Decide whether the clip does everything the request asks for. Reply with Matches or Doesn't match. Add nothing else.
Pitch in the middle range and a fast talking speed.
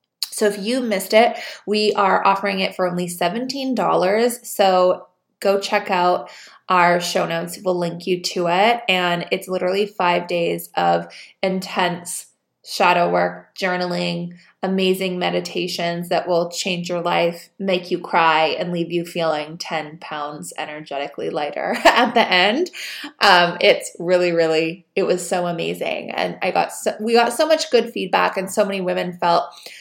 Doesn't match